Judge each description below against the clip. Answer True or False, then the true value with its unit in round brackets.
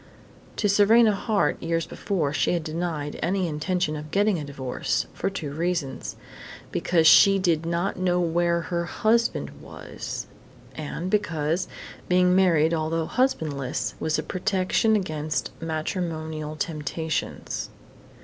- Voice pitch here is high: False (170 Hz)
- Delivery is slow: True (125 wpm)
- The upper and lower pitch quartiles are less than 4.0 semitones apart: True (3.1 semitones)